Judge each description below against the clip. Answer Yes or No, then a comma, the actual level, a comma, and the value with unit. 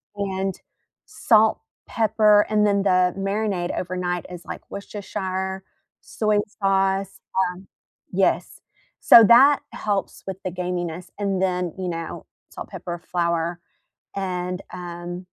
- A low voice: No, high, 190 Hz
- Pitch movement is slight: Yes, narrow, 2.1 semitones